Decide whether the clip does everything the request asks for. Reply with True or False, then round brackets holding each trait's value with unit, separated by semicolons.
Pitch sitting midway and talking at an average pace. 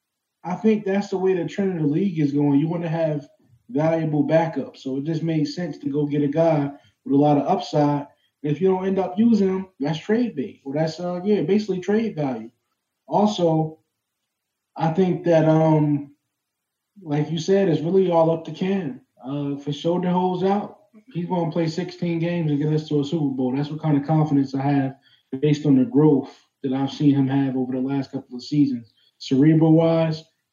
False (155 Hz; 210 wpm)